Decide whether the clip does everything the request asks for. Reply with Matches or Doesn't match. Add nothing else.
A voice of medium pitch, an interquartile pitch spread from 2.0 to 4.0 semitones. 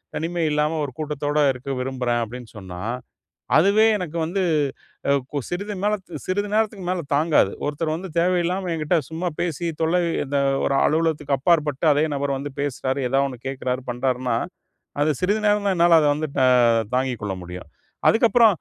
Doesn't match